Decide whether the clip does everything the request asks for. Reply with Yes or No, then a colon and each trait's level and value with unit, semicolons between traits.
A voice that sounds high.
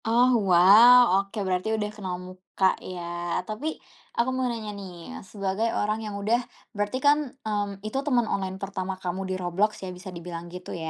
Yes: high, 200 Hz